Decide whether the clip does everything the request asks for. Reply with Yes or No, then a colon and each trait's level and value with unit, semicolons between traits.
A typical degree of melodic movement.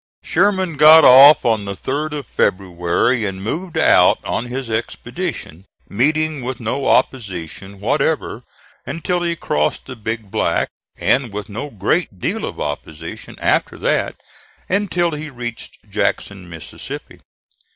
No: wide, 7.5 semitones